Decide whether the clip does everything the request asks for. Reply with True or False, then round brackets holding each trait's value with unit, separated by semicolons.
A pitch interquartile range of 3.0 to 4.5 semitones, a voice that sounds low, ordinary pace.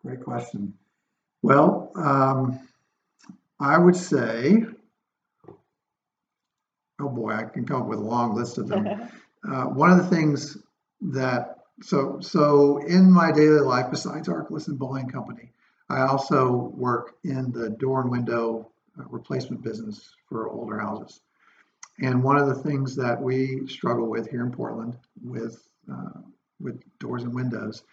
True (3.4 semitones; 130 Hz; 145 wpm)